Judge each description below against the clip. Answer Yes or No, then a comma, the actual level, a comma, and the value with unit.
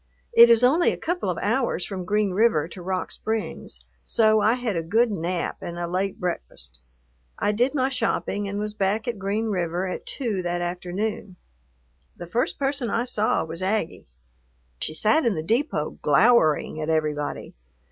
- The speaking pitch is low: No, high, 200 Hz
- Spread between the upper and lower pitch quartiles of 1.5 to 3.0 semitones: No, average, 4.7 semitones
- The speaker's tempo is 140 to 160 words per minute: No, average, 175 wpm